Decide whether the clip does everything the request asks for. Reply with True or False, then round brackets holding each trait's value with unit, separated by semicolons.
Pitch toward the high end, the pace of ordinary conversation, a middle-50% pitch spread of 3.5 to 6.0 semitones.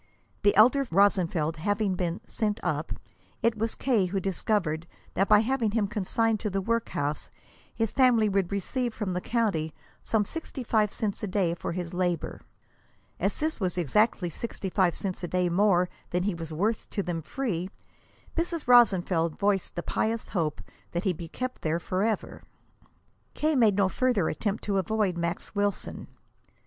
True (200 Hz; 165 wpm; 4.1 semitones)